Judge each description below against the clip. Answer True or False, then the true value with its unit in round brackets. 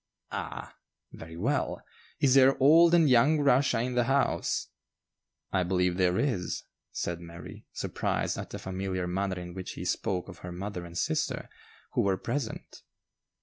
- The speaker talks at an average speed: True (155 wpm)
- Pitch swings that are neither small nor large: False (6.8 semitones)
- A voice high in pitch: False (95 Hz)